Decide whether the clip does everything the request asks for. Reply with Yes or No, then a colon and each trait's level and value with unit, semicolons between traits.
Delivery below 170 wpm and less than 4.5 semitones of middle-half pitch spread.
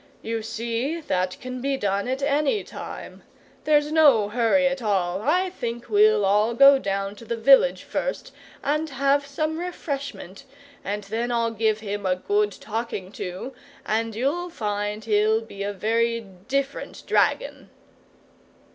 No: average, 145 wpm; average, 5.1 semitones